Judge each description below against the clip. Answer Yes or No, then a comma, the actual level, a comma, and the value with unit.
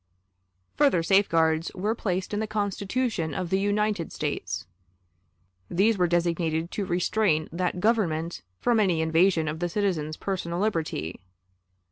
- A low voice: No, medium, 180 Hz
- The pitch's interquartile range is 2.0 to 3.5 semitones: No, average, 4.0 semitones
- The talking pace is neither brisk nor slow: No, slow, 130 wpm